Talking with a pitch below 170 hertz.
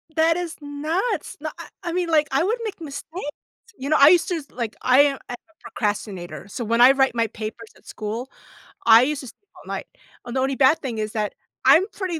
No: very high, 275 Hz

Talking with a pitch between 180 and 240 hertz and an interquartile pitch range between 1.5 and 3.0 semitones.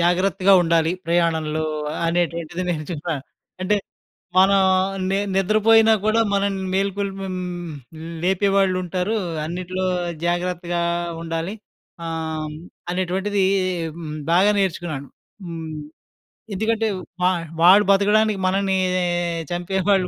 Yes: medium, 185 Hz; narrow, 2.6 semitones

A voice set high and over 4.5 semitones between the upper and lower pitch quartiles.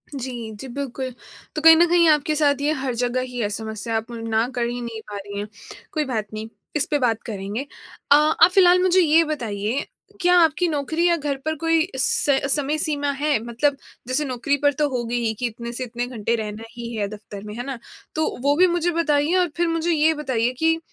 Yes: very high, 275 Hz; average, 5.0 semitones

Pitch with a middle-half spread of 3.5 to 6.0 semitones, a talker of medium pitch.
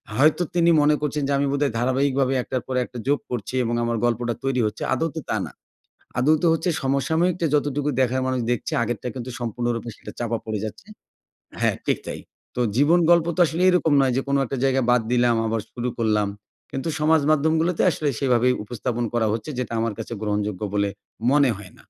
No: average, 3.9 semitones; low, 130 Hz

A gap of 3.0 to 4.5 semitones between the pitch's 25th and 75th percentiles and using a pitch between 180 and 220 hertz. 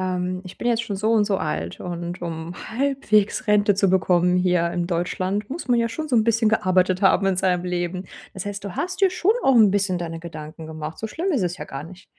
Yes: average, 3.8 semitones; medium, 185 Hz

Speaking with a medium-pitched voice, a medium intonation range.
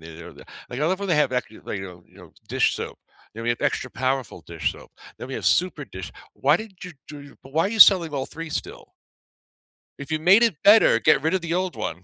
No: medium, 150 Hz; wide, 6.6 semitones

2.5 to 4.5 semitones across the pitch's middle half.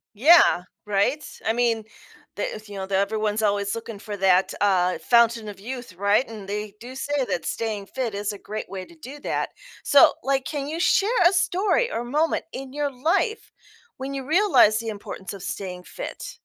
No: wide, 5.4 semitones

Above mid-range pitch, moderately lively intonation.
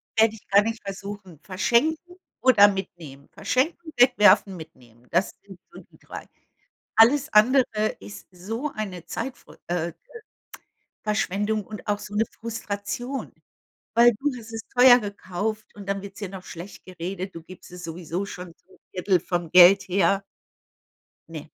Yes: high, 200 Hz; average, 3.7 semitones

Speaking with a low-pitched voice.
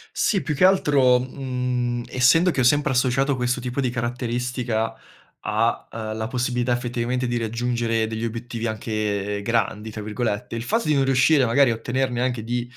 Yes: low, 120 Hz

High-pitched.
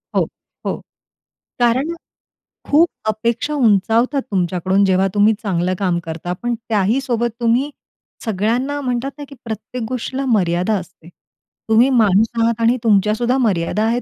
Yes: high, 225 Hz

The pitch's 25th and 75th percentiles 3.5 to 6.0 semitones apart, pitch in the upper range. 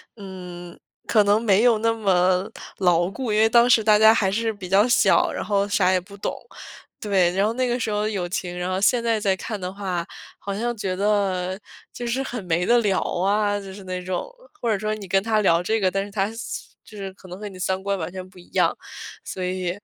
No: average, 2.7 semitones; high, 200 Hz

